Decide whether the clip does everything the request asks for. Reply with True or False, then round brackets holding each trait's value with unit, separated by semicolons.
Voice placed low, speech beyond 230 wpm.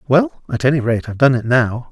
True (130 Hz; 250 wpm)